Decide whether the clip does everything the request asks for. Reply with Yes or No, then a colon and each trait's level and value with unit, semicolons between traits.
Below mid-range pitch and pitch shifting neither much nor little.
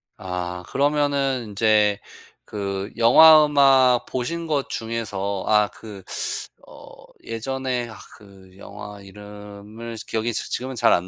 Yes: low, 110 Hz; average, 4.5 semitones